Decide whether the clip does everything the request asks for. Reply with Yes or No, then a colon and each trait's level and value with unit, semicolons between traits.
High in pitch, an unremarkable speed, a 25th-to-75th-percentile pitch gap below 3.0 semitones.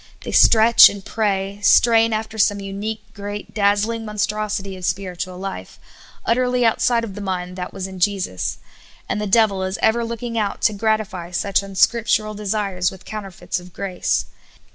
Yes: high, 205 Hz; average, 160 wpm; narrow, 2.4 semitones